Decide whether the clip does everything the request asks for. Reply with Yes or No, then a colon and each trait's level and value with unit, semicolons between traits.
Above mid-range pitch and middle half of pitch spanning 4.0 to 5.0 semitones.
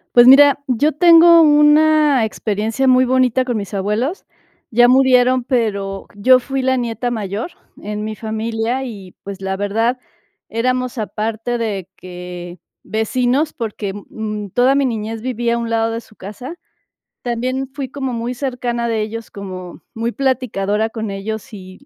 No: high, 230 Hz; average, 3.4 semitones